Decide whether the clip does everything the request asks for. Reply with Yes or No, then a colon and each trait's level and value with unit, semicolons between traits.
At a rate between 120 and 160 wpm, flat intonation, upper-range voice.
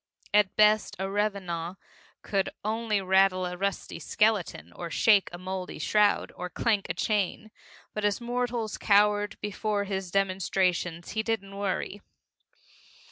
Yes: slow, 135 wpm; narrow, 2.2 semitones; high, 200 Hz